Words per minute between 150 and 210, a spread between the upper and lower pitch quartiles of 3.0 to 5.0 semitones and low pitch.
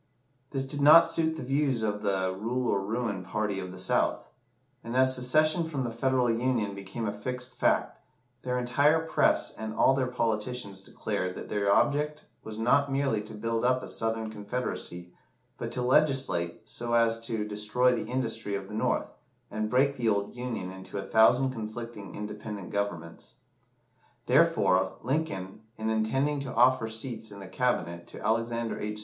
Yes: average, 170 wpm; average, 3.7 semitones; low, 115 Hz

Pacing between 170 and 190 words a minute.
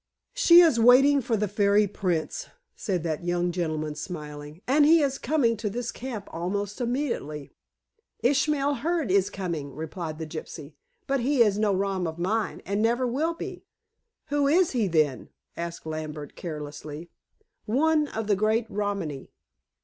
No: average, 155 wpm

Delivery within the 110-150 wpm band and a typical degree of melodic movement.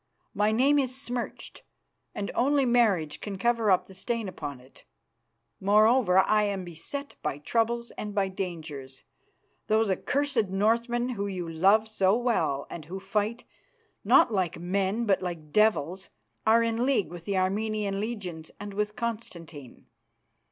Yes: average, 145 wpm; average, 4.1 semitones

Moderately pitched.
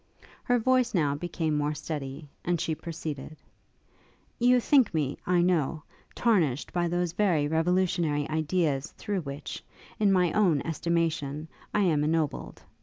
Yes: medium, 165 Hz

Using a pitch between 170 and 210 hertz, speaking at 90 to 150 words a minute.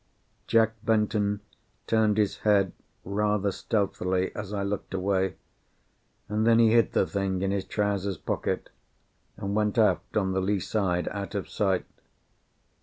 No: low, 100 Hz; average, 145 wpm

